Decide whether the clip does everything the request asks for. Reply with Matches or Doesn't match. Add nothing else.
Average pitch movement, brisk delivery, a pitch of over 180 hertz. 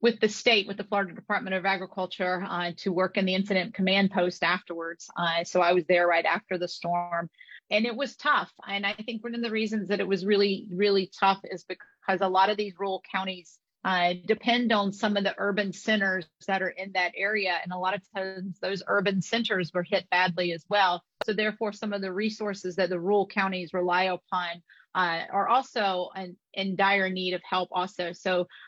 Doesn't match